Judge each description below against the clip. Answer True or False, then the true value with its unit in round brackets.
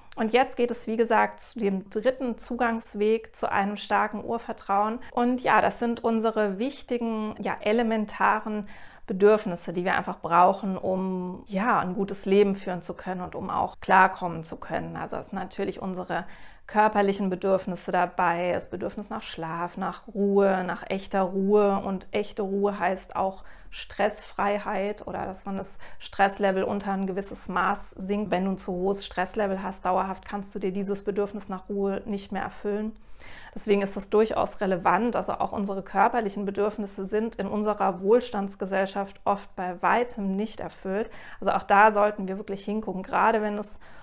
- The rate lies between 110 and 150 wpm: False (165 wpm)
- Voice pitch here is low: False (200 Hz)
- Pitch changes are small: True (2.0 semitones)